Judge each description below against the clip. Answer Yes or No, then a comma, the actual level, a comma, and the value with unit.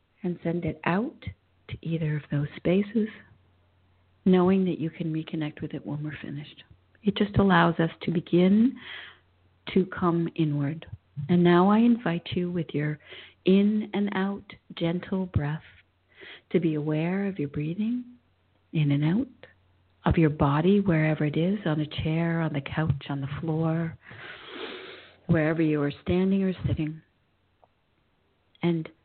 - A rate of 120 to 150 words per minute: Yes, average, 145 wpm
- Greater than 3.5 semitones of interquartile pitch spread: Yes, average, 3.9 semitones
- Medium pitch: Yes, medium, 160 Hz